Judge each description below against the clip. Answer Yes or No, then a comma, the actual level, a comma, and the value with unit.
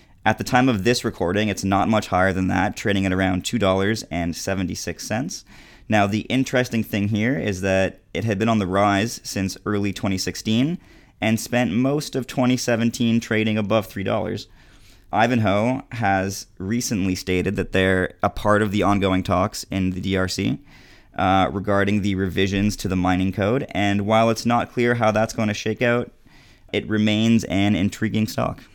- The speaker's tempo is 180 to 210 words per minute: No, average, 165 wpm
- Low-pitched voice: Yes, low, 105 Hz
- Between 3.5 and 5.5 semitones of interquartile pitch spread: No, average, 3.1 semitones